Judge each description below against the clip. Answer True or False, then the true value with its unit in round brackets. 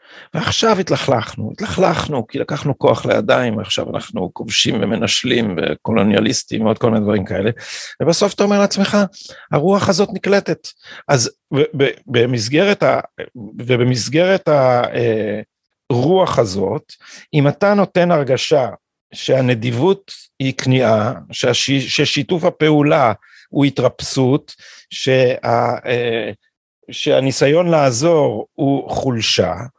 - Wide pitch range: True (6.6 semitones)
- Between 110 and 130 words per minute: False (100 wpm)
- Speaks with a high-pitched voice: False (140 Hz)